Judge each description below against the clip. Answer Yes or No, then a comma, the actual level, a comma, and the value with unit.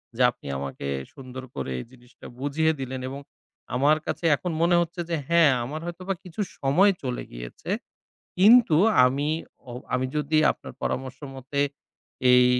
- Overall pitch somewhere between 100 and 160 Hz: Yes, medium, 140 Hz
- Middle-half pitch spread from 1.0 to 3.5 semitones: No, average, 4.8 semitones